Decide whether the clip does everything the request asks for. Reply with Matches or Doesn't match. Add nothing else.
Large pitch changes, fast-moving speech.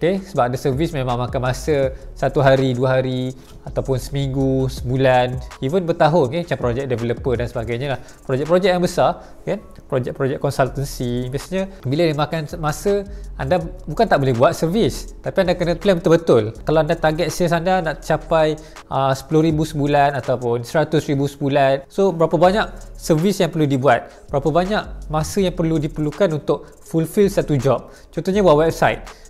Doesn't match